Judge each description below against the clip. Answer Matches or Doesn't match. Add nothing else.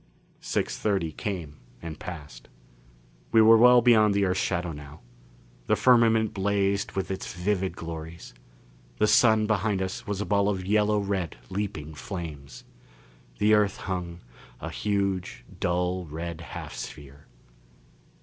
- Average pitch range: Matches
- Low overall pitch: Matches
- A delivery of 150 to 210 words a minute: Doesn't match